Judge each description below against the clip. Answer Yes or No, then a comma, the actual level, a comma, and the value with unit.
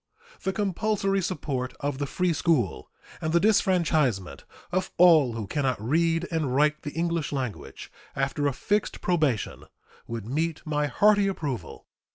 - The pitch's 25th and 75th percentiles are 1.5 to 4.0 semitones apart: No, average, 5.2 semitones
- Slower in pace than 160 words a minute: Yes, average, 150 wpm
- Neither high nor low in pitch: Yes, medium, 155 Hz